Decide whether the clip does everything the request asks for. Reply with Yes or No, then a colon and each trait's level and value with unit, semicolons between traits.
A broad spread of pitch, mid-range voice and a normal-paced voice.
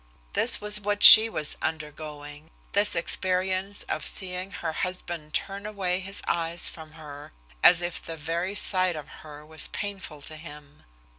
No: average, 3.8 semitones; medium, 170 Hz; average, 155 wpm